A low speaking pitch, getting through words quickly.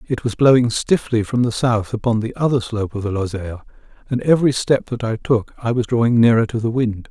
Yes: low, 115 Hz; fast, 230 wpm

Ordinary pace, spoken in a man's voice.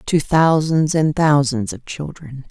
No: average, 145 wpm; female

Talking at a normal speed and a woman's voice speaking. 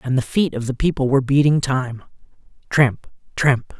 No: average, 160 wpm; male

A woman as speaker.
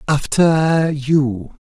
No: male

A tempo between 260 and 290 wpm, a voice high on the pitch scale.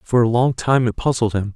No: fast, 270 wpm; low, 120 Hz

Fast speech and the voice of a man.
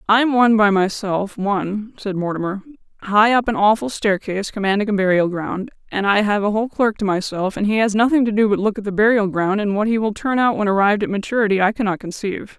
No: fast, 240 wpm; female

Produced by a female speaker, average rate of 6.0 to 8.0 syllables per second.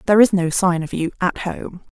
No: female; 5.6 syllables/s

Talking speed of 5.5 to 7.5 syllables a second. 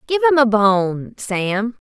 No: 3.4 syllables/s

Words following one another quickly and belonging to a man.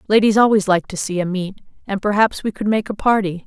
No: fast, 240 wpm; female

